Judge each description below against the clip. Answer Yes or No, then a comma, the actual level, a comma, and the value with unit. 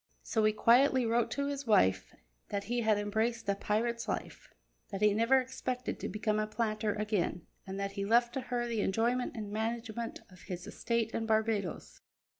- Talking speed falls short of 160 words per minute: No, average, 185 wpm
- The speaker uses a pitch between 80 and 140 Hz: No, high, 220 Hz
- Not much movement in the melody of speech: Yes, narrow, 2.3 semitones